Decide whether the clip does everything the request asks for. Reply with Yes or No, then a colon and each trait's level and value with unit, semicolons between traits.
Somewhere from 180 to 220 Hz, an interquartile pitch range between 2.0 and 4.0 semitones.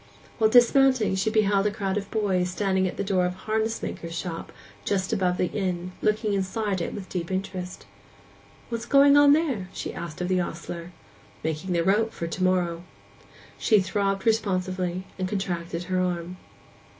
Yes: high, 190 Hz; average, 2.9 semitones